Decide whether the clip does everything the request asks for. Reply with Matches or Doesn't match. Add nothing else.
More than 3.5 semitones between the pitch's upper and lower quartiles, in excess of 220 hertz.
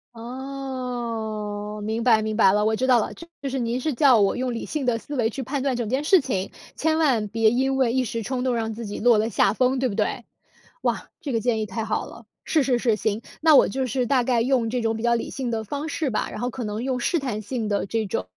Doesn't match